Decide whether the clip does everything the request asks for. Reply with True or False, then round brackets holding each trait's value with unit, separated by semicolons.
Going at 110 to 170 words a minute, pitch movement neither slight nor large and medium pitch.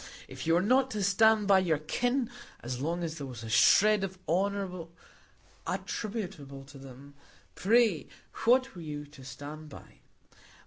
False (160 wpm; 6.6 semitones; 175 Hz)